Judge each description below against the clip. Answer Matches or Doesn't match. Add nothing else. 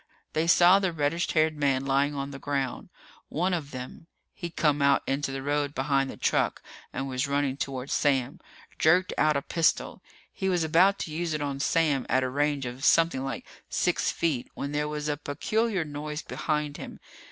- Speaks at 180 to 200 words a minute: Matches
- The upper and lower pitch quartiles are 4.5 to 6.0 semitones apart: Doesn't match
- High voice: Doesn't match